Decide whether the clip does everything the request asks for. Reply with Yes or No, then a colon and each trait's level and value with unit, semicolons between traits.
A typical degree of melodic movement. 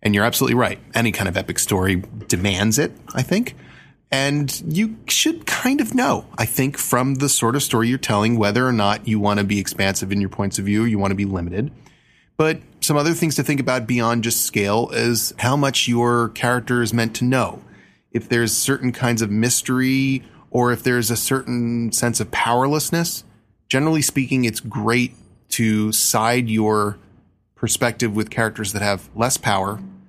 Yes: average, 3.6 semitones